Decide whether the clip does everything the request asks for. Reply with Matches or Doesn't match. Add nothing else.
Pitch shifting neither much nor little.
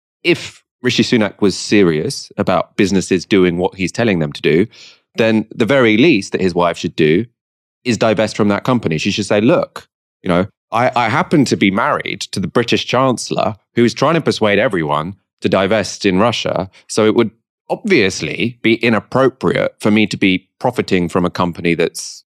Matches